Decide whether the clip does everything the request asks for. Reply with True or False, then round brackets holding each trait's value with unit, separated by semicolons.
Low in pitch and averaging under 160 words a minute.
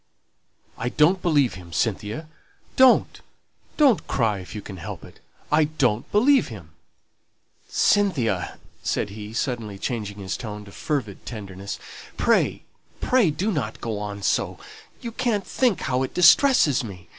True (120 Hz; 145 wpm)